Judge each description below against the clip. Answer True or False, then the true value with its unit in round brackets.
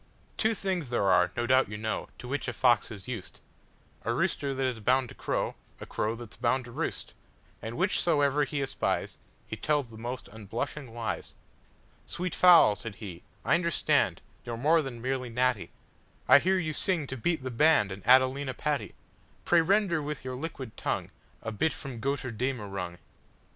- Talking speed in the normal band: True (155 wpm)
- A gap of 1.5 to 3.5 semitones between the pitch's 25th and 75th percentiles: False (4.7 semitones)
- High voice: False (130 Hz)